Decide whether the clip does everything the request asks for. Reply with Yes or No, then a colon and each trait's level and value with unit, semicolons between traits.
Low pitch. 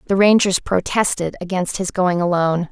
No: medium, 185 Hz